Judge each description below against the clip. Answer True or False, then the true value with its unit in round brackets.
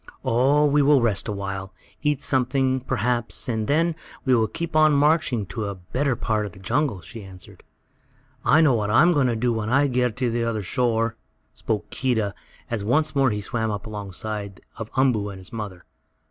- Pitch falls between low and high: False (115 Hz)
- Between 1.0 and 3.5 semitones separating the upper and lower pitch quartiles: False (4.5 semitones)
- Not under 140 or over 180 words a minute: False (200 wpm)